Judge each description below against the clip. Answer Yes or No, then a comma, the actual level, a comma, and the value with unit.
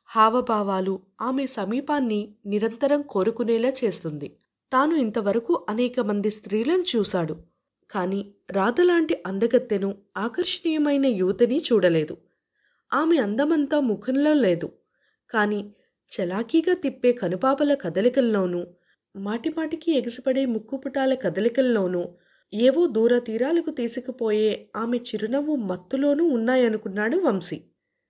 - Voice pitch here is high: Yes, high, 235 Hz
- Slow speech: No, average, 85 wpm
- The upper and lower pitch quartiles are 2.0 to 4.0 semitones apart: No, average, 5.2 semitones